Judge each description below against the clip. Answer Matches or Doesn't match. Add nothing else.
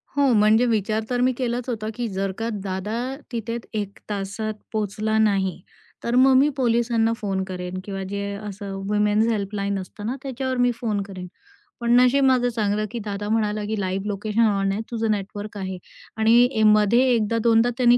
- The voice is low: Doesn't match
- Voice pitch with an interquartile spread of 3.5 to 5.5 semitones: Doesn't match